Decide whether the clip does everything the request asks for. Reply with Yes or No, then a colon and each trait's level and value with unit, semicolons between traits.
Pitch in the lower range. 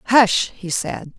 No: high, 200 Hz